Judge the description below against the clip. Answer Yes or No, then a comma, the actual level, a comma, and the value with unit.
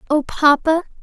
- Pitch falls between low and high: No, very high, 305 Hz